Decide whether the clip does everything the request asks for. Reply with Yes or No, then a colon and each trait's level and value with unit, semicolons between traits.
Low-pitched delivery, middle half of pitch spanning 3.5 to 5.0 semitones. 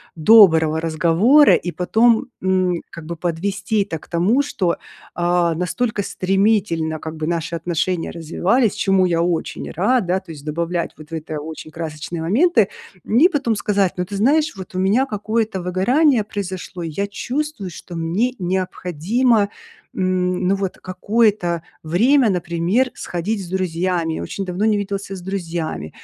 No: medium, 185 Hz; average, 3.8 semitones